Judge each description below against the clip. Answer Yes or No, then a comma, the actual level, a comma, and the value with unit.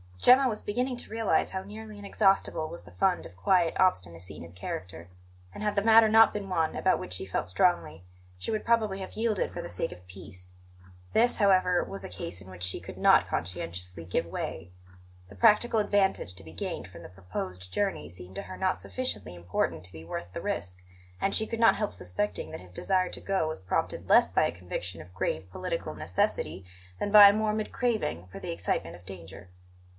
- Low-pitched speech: Yes, low, 105 Hz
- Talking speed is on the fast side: Yes, fast, 210 wpm